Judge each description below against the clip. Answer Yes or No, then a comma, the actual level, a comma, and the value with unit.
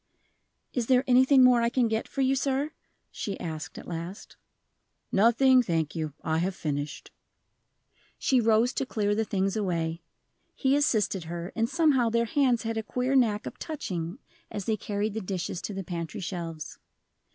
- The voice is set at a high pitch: Yes, high, 215 Hz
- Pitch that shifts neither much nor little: No, wide, 6.2 semitones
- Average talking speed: Yes, average, 170 wpm